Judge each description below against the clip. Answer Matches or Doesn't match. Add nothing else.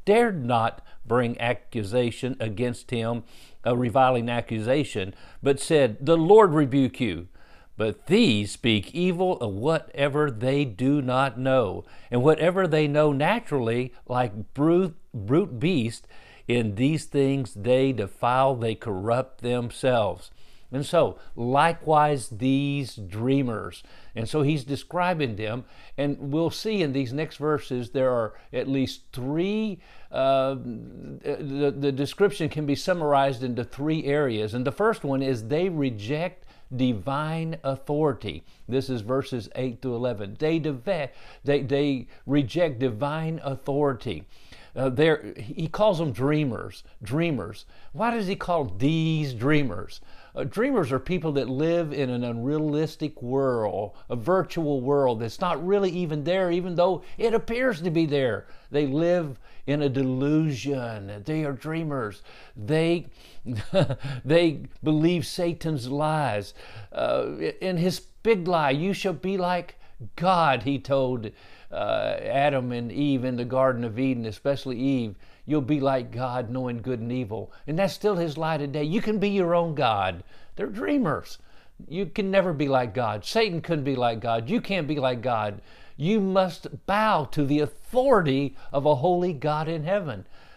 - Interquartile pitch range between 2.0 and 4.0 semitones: Doesn't match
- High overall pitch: Doesn't match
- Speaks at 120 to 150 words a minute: Matches